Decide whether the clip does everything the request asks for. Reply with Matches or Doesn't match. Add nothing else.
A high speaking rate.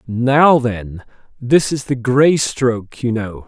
Doesn't match